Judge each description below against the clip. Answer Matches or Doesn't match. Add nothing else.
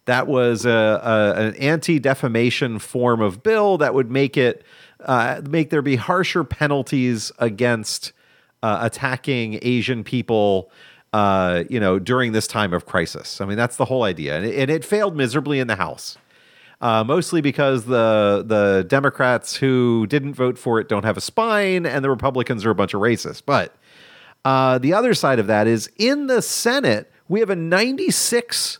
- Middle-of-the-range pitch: Doesn't match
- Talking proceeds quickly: Doesn't match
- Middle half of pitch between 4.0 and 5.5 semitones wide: Matches